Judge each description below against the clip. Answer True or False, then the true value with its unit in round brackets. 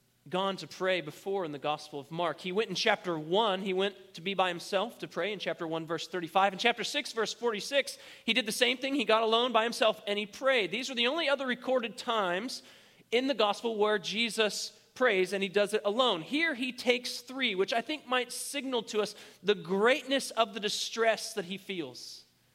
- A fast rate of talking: True (220 wpm)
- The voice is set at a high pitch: True (215 Hz)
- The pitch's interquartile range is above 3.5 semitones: True (4.3 semitones)